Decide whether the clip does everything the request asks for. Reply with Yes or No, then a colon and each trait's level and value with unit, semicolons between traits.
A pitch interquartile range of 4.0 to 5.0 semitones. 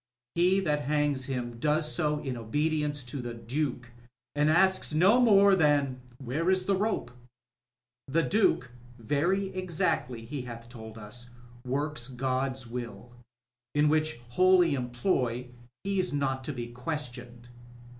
Yes: average, 4.7 semitones